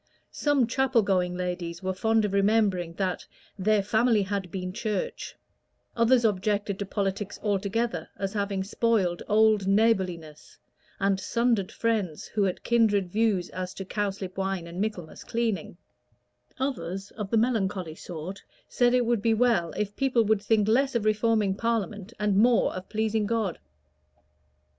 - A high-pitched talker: Yes, high, 205 Hz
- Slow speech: No, average, 150 wpm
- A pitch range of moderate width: Yes, average, 3.1 semitones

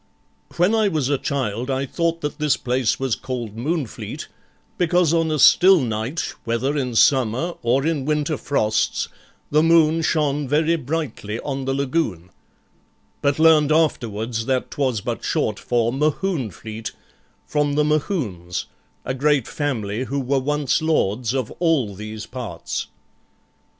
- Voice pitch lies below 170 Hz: Yes, medium, 140 Hz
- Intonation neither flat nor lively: Yes, average, 4.7 semitones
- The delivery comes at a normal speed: Yes, average, 145 wpm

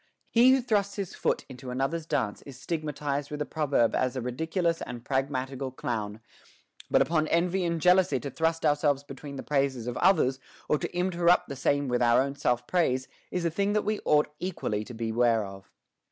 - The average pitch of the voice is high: No, medium, 145 Hz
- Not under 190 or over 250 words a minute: Yes, average, 195 wpm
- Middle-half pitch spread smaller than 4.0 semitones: No, average, 4.9 semitones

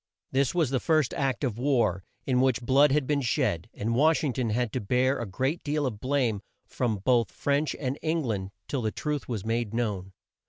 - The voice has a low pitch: Yes, low, 125 Hz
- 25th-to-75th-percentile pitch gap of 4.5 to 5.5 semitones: No, average, 4.0 semitones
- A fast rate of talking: Yes, fast, 210 wpm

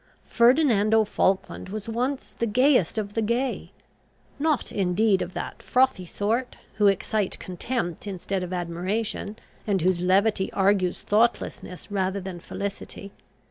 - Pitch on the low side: No, high, 205 Hz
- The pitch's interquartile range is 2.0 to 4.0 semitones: Yes, average, 3.5 semitones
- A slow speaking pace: Yes, slow, 130 wpm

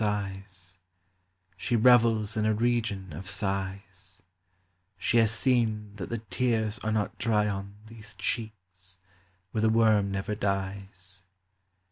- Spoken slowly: Yes, slow, 125 wpm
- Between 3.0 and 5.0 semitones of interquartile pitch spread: No, narrow, 2.4 semitones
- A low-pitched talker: Yes, low, 105 Hz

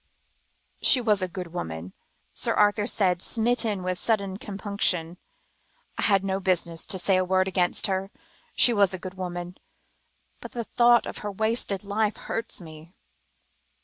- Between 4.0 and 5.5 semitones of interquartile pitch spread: No, narrow, 2.6 semitones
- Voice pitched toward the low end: No, high, 190 Hz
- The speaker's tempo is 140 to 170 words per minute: Yes, average, 155 wpm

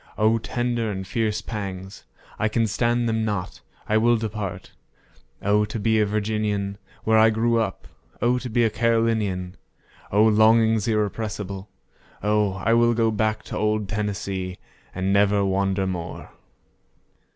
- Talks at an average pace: No, slow, 130 wpm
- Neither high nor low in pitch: No, low, 105 Hz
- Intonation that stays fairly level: Yes, narrow, 2.2 semitones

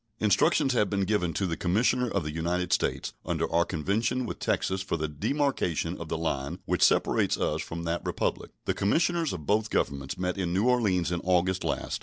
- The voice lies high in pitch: No, very low, 90 Hz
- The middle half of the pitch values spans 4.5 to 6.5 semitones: No, average, 4.1 semitones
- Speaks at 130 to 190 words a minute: No, average, 200 wpm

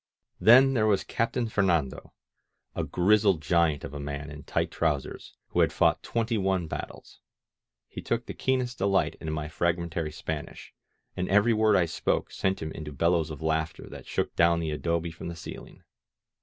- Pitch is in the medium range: No, very low, 85 Hz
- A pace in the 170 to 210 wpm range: Yes, average, 180 wpm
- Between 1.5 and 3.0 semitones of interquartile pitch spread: No, average, 4.5 semitones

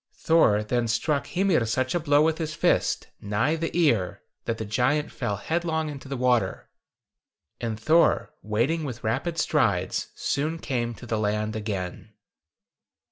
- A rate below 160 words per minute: Yes, average, 150 wpm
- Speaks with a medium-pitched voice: No, low, 125 Hz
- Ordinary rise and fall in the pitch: No, wide, 6.2 semitones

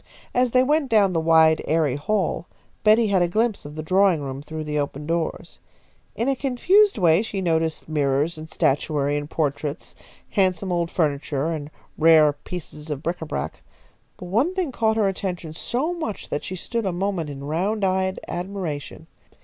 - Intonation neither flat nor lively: Yes, average, 5.0 semitones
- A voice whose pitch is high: No, medium, 170 Hz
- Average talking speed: Yes, average, 175 wpm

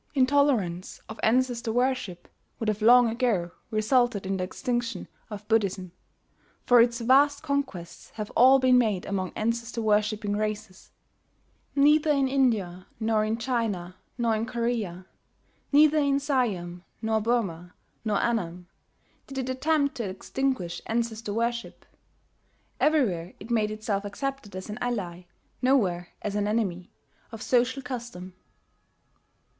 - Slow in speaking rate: Yes, slow, 130 wpm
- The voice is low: No, high, 225 Hz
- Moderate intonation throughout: Yes, average, 4.2 semitones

